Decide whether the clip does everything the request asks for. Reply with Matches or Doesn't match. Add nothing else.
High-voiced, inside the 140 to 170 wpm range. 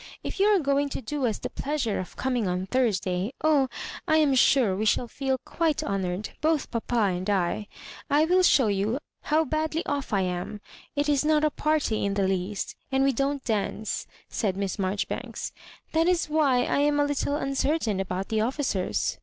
Doesn't match